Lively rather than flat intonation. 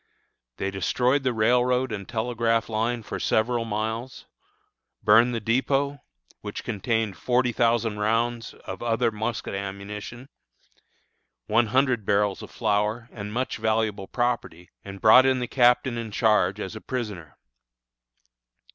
No: narrow, 2.6 semitones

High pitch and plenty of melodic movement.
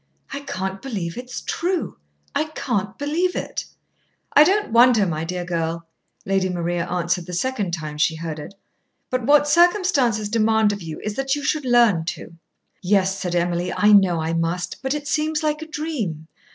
Yes: high, 205 Hz; wide, 8.4 semitones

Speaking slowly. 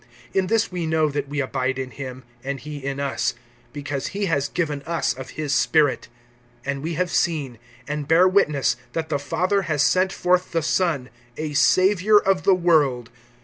No: average, 185 wpm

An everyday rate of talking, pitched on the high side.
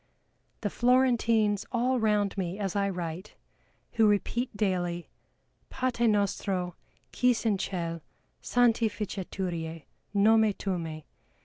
No: slow, 105 wpm; high, 205 Hz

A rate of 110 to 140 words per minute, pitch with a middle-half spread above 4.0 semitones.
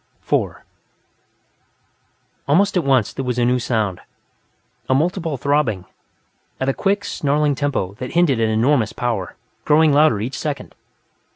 Yes: slow, 135 wpm; average, 4.6 semitones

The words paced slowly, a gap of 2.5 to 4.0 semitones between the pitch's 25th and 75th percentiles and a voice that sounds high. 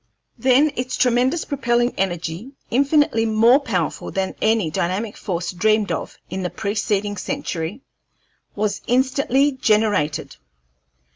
No: slow, 115 wpm; average, 5.0 semitones; high, 220 Hz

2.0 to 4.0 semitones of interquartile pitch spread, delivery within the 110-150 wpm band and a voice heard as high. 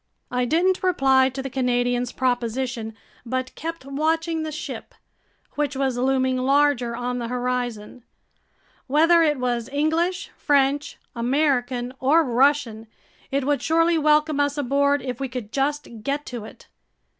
Yes: average, 3.1 semitones; average, 140 wpm; very high, 270 Hz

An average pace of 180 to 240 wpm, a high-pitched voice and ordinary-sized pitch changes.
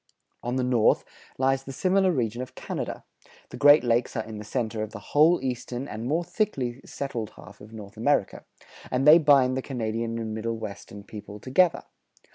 No: average, 185 wpm; low, 120 Hz; average, 3.8 semitones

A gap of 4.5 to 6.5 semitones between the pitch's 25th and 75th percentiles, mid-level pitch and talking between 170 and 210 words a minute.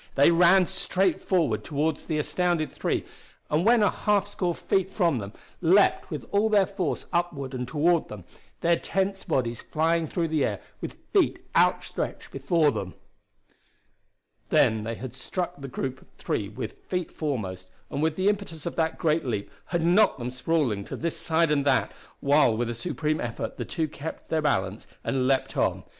Yes: average, 5.1 semitones; medium, 155 Hz; average, 180 wpm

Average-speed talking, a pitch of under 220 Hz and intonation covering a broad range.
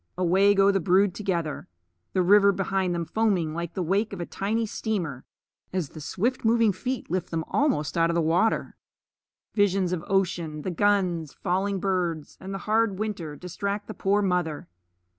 No: average, 170 wpm; high, 190 Hz; average, 3.0 semitones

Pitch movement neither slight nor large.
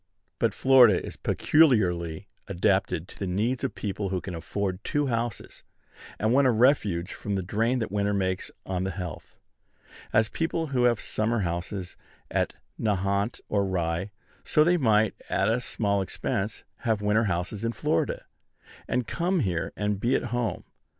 Yes: average, 3.9 semitones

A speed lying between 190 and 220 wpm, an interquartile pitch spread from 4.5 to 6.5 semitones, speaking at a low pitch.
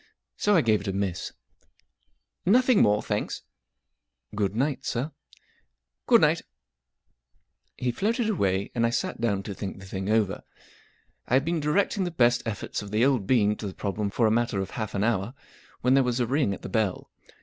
Yes: fast, 205 wpm; average, 5.0 semitones; low, 110 Hz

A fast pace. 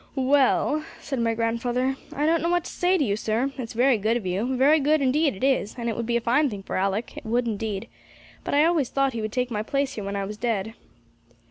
Yes: fast, 255 wpm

